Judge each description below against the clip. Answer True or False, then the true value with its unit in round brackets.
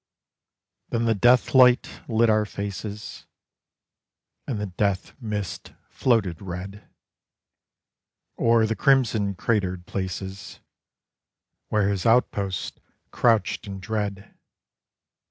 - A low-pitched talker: True (105 Hz)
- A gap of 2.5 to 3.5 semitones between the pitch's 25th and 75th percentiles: True (2.8 semitones)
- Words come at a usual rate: False (95 wpm)